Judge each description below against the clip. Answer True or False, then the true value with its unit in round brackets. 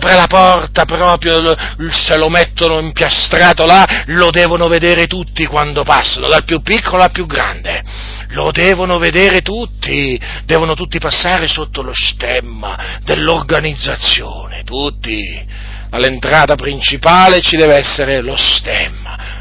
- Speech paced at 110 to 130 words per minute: True (125 wpm)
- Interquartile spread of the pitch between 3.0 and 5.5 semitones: True (5.1 semitones)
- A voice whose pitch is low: False (160 Hz)